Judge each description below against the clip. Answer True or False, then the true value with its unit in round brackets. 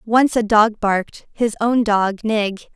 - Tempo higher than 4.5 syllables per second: False (4.2 syllables/s)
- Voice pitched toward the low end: False (220 Hz)